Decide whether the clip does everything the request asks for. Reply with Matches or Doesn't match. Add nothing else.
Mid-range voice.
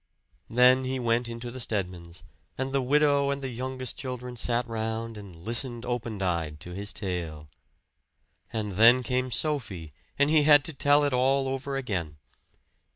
Doesn't match